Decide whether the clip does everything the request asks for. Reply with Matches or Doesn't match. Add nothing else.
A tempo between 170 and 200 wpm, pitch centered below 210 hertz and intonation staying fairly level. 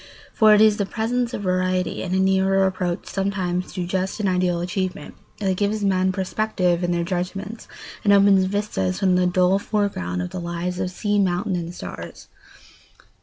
Matches